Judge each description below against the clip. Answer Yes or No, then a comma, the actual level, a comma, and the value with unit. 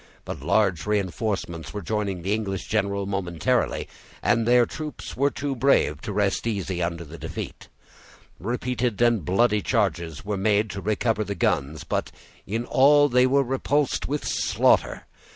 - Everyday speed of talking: Yes, average, 150 wpm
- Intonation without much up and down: No, average, 4.1 semitones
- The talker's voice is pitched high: No, low, 105 Hz